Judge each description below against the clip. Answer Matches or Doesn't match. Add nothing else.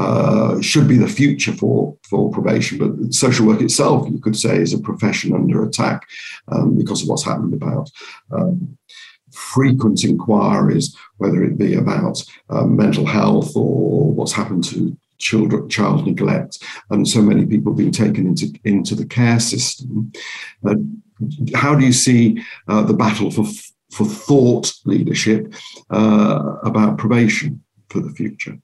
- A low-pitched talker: Matches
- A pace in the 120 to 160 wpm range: Matches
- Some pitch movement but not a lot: Matches